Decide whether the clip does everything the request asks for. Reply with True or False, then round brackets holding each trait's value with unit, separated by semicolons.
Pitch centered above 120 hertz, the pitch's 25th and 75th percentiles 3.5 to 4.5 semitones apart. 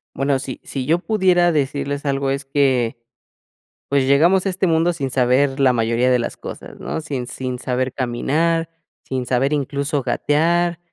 True (140 Hz; 3.9 semitones)